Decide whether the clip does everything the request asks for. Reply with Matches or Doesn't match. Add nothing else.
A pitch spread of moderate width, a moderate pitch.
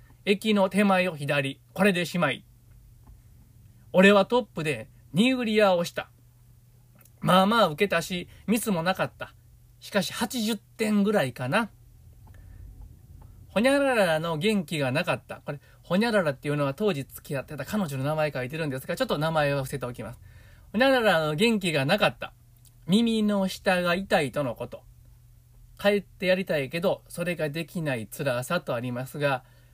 Doesn't match